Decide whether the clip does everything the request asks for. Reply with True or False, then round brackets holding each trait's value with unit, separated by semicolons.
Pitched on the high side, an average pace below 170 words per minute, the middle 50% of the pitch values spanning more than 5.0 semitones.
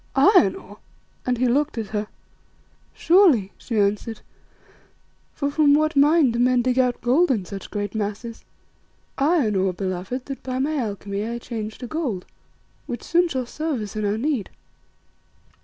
True (245 Hz; 160 wpm; 5.5 semitones)